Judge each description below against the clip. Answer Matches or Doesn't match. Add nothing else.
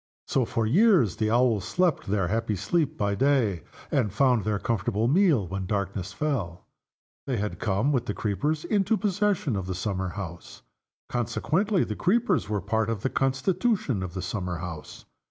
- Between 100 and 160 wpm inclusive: Doesn't match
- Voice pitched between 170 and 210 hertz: Doesn't match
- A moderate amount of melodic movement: Doesn't match